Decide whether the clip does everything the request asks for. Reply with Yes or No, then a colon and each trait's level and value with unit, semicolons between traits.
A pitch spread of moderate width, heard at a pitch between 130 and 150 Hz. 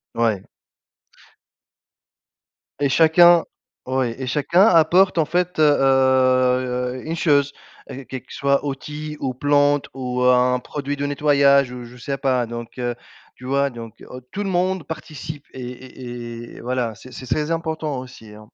Yes: average, 3.1 semitones; low, 135 Hz